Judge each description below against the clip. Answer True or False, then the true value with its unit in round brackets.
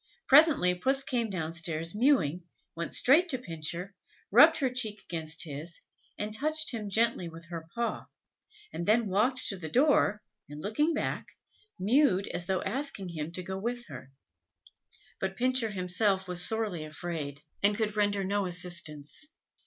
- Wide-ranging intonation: True (5.9 semitones)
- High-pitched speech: True (195 Hz)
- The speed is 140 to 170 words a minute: True (155 wpm)